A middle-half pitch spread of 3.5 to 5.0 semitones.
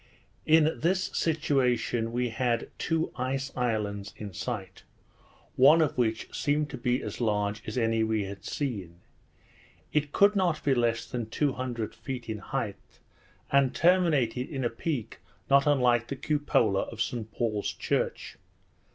Yes: average, 4.4 semitones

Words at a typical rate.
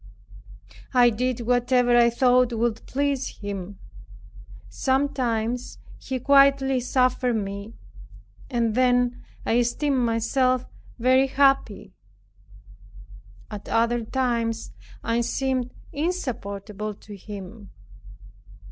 No: slow, 90 wpm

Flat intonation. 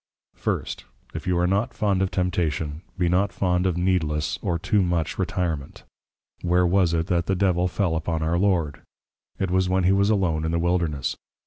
Yes: narrow, 2.2 semitones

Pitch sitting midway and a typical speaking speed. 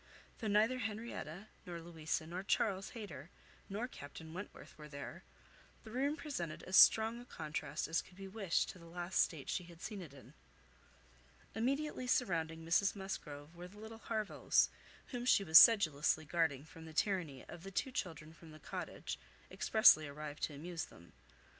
Yes: medium, 175 Hz; average, 170 wpm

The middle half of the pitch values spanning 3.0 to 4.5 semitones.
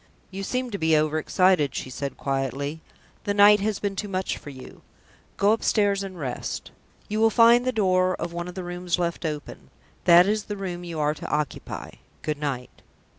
No: average, 5.0 semitones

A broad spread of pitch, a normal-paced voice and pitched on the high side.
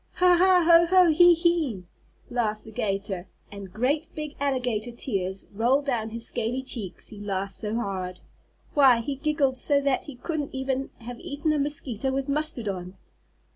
Yes: wide, 5.8 semitones; average, 170 wpm; very high, 255 Hz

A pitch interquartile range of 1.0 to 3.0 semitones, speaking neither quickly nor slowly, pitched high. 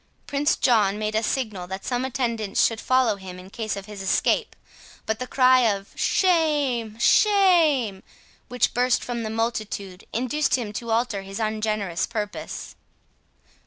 No: average, 3.7 semitones; average, 150 wpm; high, 225 Hz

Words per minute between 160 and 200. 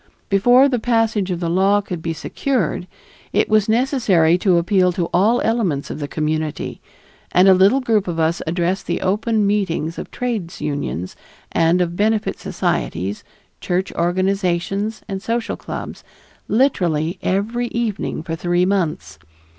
No: average, 145 wpm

